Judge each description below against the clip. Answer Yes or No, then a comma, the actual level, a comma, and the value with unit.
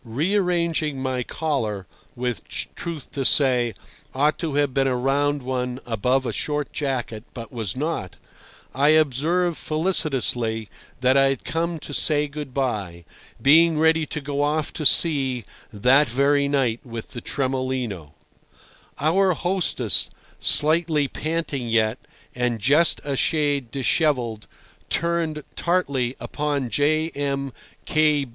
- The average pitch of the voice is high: No, medium, 140 Hz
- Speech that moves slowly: Yes, slow, 125 wpm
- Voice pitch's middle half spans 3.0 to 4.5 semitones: Yes, average, 3.8 semitones